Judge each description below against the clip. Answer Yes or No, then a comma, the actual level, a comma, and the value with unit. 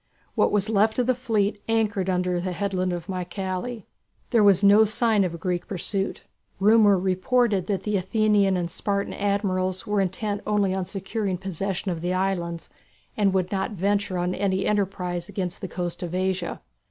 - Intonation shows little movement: Yes, narrow, 2.2 semitones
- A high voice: Yes, high, 195 Hz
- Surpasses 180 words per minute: No, average, 175 wpm